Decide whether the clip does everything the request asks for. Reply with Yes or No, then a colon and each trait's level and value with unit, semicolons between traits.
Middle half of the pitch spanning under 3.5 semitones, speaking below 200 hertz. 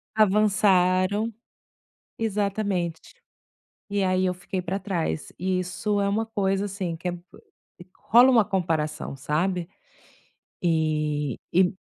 Yes: average, 3.0 semitones; medium, 185 Hz